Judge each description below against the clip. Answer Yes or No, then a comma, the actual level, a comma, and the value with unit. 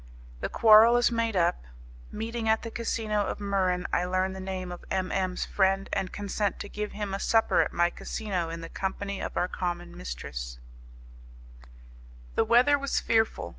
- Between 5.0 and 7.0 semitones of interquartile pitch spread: No, average, 3.5 semitones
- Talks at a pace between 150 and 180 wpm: Yes, average, 175 wpm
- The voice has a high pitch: Yes, high, 195 Hz